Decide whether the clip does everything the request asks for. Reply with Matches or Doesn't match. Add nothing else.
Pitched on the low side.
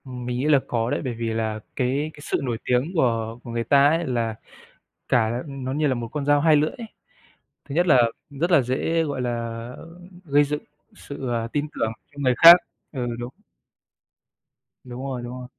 Matches